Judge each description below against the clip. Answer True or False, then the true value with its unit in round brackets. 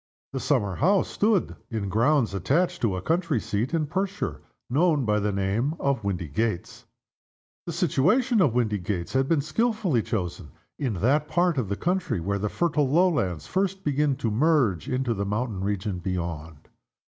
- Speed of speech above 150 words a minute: True (160 wpm)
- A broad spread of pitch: True (8.5 semitones)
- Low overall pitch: True (125 Hz)